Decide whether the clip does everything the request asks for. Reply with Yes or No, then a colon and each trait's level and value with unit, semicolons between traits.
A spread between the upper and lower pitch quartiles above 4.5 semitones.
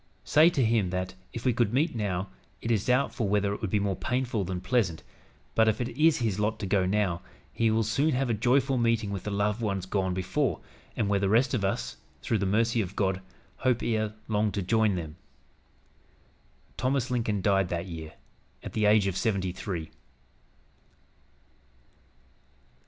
No: average, 3.6 semitones